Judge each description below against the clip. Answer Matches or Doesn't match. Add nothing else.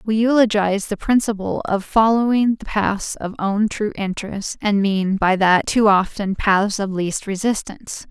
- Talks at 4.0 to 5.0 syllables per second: Matches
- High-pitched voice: Matches